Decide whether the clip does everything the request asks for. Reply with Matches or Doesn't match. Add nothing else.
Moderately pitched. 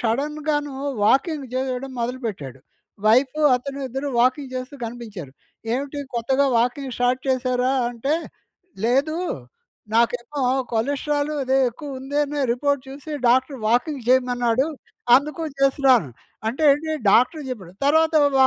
Doesn't match